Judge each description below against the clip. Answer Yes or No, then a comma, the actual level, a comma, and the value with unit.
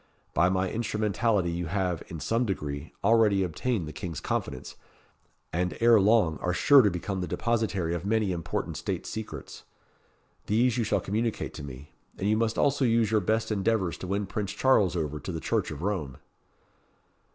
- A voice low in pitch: Yes, low, 100 Hz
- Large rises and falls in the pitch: No, average, 4.5 semitones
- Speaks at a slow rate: No, average, 175 wpm